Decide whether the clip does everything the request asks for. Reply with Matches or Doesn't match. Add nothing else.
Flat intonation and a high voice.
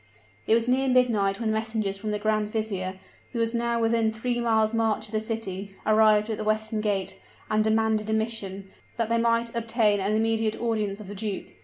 Matches